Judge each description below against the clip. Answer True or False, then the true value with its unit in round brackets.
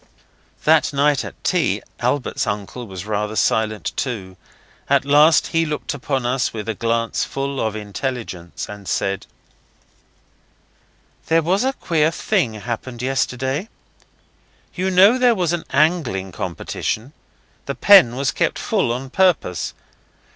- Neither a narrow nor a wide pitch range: False (6.5 semitones)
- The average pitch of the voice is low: True (130 Hz)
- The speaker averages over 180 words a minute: False (135 wpm)